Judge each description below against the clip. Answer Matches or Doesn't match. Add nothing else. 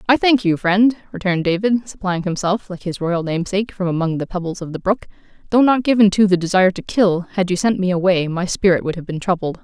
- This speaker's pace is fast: Matches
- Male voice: Doesn't match